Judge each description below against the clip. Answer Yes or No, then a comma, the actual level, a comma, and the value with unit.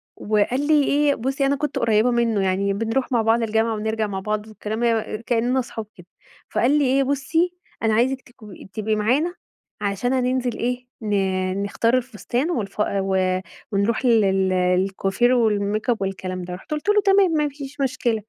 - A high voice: Yes, high, 230 Hz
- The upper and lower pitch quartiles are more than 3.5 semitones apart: Yes, average, 4.2 semitones